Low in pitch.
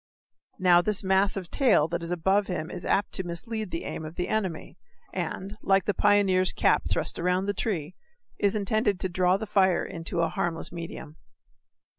No: medium, 185 Hz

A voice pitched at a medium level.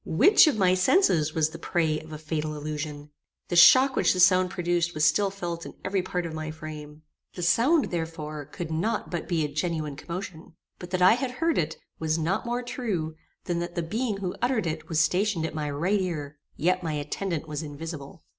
Yes: medium, 170 Hz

